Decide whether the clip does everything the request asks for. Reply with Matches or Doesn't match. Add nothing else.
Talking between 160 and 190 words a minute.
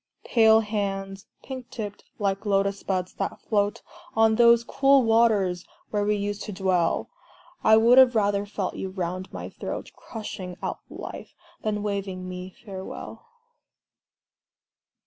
Doesn't match